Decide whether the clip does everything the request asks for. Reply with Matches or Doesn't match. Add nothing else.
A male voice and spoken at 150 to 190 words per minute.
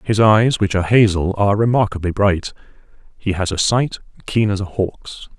Matches